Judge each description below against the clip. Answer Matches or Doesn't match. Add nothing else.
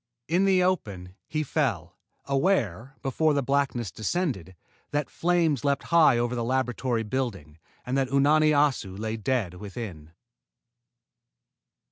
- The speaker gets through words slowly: Matches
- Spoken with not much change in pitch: Doesn't match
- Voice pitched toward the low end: Matches